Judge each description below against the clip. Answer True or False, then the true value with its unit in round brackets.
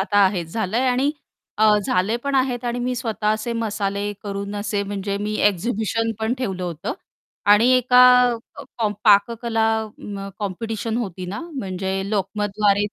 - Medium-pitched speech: False (210 Hz)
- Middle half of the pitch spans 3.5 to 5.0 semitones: False (2.9 semitones)